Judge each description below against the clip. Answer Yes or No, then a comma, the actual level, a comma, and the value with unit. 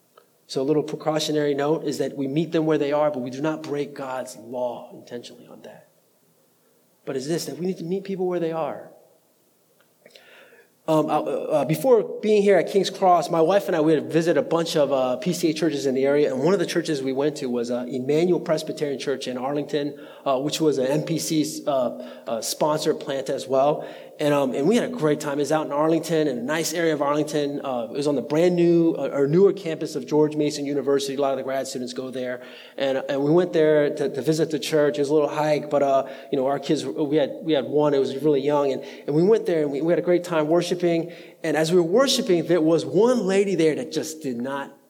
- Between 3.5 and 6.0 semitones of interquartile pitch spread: No, average, 3.0 semitones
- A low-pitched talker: No, medium, 150 Hz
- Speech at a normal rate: No, fast, 245 wpm